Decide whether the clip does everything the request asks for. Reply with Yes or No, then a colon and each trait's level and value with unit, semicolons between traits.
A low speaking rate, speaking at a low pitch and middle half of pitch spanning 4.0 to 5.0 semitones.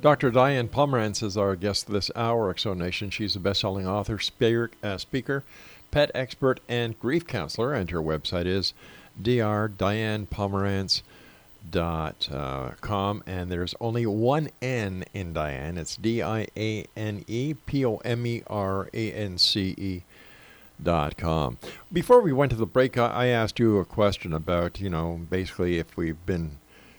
No: average, 145 wpm; low, 105 Hz; average, 4.7 semitones